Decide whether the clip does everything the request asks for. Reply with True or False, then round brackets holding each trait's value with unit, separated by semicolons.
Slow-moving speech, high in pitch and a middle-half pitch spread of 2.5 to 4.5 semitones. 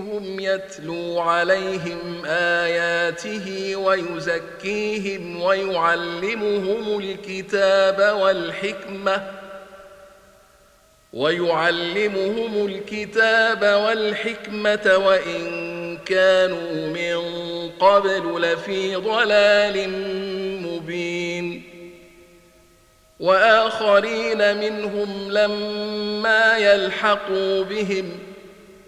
True (45 wpm; 195 Hz; 2.9 semitones)